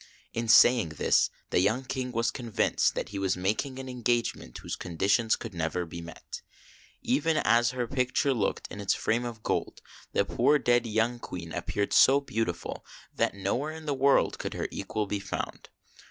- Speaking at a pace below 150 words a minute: No, average, 180 wpm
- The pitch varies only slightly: No, average, 4.4 semitones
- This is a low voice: Yes, low, 115 Hz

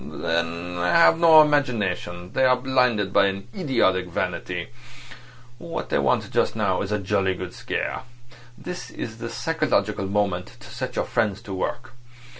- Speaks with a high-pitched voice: No, low, 105 Hz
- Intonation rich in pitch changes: Yes, wide, 5.8 semitones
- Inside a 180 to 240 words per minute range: No, average, 155 wpm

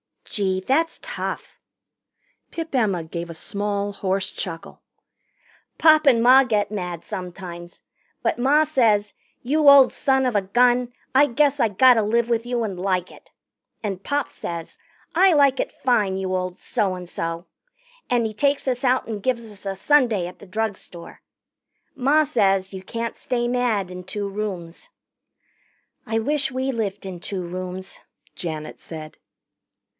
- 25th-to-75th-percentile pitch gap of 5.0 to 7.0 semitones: Yes, wide, 5.4 semitones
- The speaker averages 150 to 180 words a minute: Yes, average, 155 wpm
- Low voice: No, high, 215 Hz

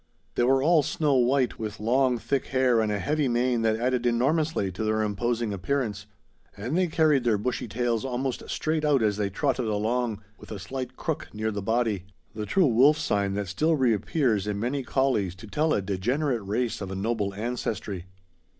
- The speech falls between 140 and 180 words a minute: No, average, 190 wpm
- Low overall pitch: Yes, low, 120 Hz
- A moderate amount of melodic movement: Yes, average, 4.3 semitones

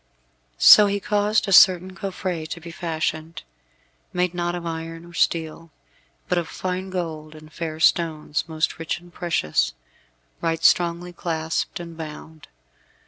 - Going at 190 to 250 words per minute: No, average, 140 wpm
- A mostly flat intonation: Yes, narrow, 1.9 semitones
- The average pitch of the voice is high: No, medium, 170 Hz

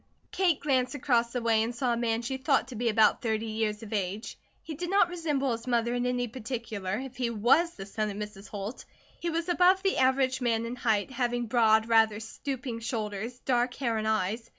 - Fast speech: Yes, fast, 215 wpm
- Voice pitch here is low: No, high, 235 Hz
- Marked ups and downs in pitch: No, average, 2.9 semitones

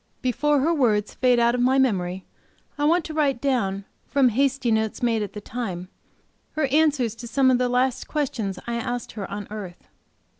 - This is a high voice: Yes, high, 245 Hz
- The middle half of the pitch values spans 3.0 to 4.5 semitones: Yes, average, 4.2 semitones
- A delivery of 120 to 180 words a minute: No, average, 190 wpm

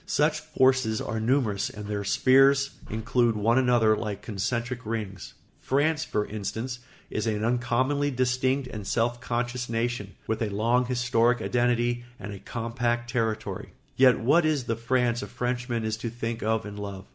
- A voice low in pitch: Yes, low, 120 Hz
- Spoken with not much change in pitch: Yes, narrow, 2.3 semitones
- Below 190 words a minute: Yes, average, 160 wpm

